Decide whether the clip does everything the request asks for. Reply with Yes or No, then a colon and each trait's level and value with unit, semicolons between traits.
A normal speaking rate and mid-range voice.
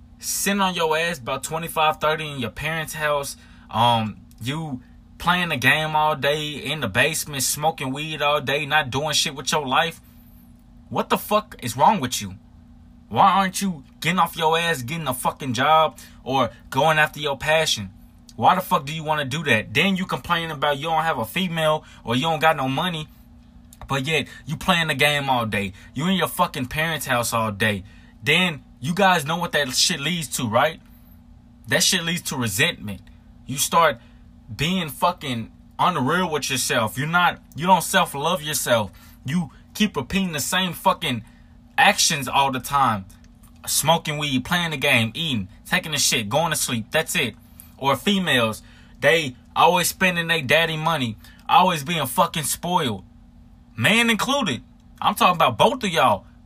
Yes: average, 175 wpm; medium, 150 Hz